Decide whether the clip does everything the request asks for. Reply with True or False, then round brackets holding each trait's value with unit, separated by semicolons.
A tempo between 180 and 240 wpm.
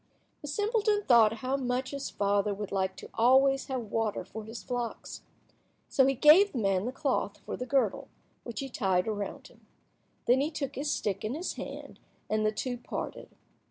True (190 wpm)